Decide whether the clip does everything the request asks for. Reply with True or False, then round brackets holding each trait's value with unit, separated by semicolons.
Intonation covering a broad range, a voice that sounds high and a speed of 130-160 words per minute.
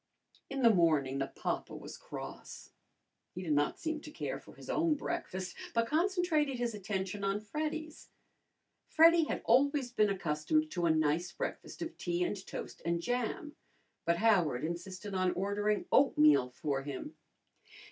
True (9.0 semitones; 200 Hz; 155 wpm)